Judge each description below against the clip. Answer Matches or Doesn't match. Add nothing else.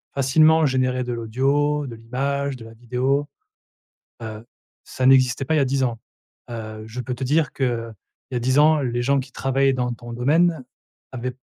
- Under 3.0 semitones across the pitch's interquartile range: Matches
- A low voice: Matches